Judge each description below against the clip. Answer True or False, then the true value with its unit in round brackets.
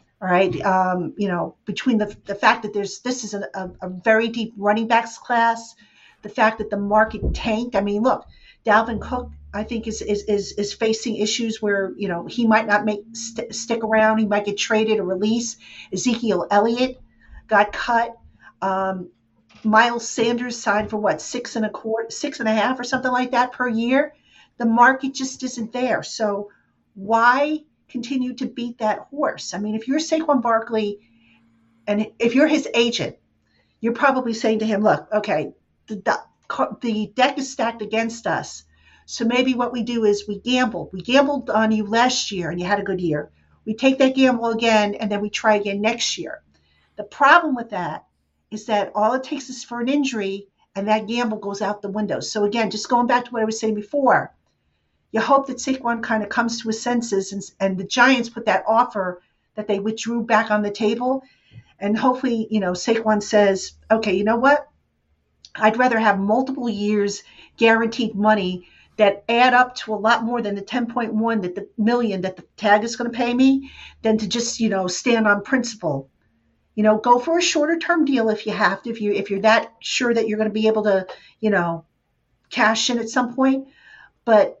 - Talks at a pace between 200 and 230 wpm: True (205 wpm)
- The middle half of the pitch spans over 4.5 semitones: False (2.9 semitones)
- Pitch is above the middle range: True (220 Hz)